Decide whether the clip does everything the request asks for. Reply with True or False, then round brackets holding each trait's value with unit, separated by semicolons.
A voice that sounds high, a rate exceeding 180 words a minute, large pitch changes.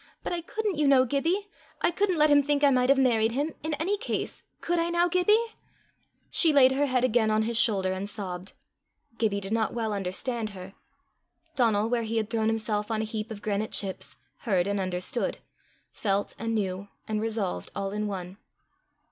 True (225 Hz; 195 wpm; 5.8 semitones)